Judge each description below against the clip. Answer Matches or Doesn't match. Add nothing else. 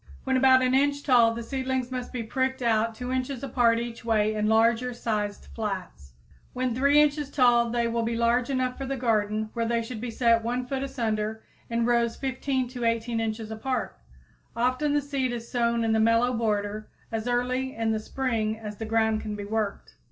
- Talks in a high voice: Matches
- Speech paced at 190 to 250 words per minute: Matches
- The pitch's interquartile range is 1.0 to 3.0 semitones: Matches